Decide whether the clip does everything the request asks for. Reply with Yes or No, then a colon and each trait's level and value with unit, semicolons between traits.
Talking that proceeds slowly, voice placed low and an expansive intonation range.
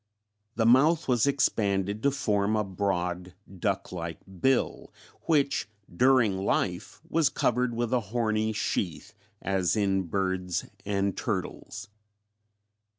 No: slow, 115 wpm; low, 105 Hz; average, 4.4 semitones